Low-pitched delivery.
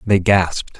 Yes: very low, 95 Hz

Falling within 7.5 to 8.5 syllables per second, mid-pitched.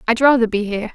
No: 7.6 syllables/s; high, 230 Hz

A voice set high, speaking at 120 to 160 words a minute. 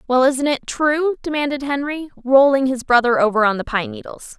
No: very high, 265 Hz; average, 190 wpm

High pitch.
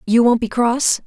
Yes: high, 235 Hz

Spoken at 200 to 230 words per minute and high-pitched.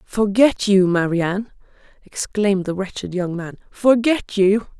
No: average, 140 wpm; high, 200 Hz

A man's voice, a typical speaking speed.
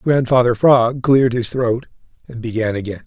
Yes: male; average, 155 wpm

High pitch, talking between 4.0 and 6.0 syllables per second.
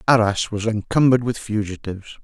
No: low, 110 Hz; 5.9 syllables/s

